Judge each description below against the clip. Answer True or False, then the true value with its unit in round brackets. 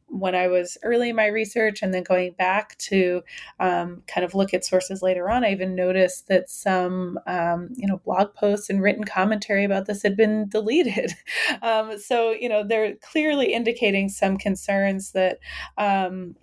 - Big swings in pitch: False (2.7 semitones)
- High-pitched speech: True (195 Hz)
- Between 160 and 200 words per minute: True (180 wpm)